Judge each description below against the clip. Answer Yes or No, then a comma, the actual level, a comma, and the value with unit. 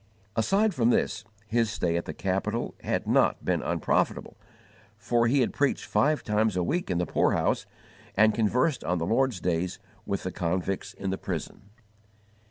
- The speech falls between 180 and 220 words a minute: No, average, 170 wpm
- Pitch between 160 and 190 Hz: No, low, 110 Hz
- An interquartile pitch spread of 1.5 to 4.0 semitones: No, average, 5.2 semitones